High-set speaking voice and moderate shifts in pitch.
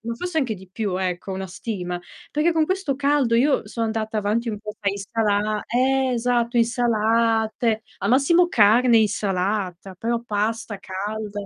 Yes: high, 225 Hz; average, 3.0 semitones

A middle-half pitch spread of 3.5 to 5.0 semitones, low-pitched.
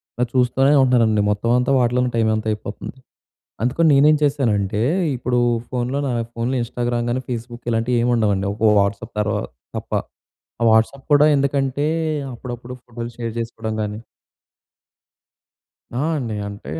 No: narrow, 2.5 semitones; low, 120 Hz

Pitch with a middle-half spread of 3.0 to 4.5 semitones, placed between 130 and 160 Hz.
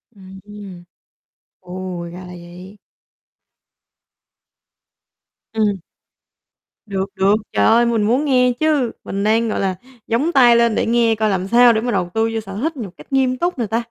No: average, 3.9 semitones; high, 220 Hz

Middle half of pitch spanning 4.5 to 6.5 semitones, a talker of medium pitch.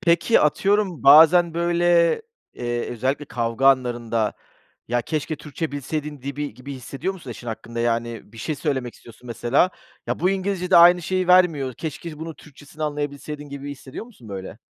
Yes: wide, 5.6 semitones; medium, 145 Hz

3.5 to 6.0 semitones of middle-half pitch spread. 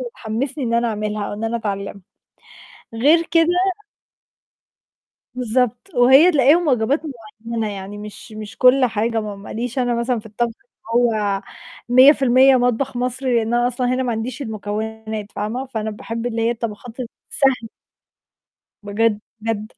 No: average, 2.9 semitones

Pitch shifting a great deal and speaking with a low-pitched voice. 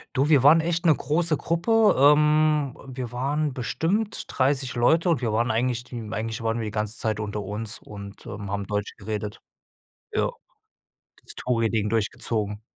Yes: wide, 5.9 semitones; low, 120 Hz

